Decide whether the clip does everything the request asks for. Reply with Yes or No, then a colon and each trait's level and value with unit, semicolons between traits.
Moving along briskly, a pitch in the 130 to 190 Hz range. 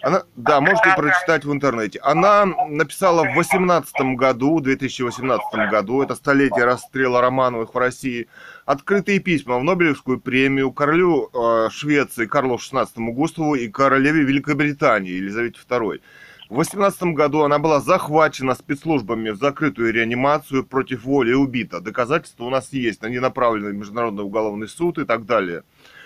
No: average, 140 wpm; low, 135 Hz